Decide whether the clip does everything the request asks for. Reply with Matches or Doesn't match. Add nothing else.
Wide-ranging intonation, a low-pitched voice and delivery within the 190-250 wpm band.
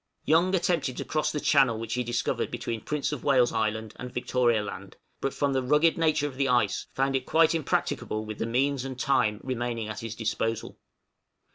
Doesn't match